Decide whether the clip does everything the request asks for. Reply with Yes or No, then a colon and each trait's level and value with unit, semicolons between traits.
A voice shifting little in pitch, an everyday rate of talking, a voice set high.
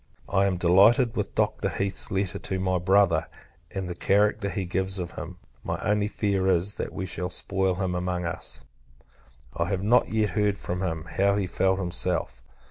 No: narrow, 2.0 semitones; average, 185 wpm; very low, 95 Hz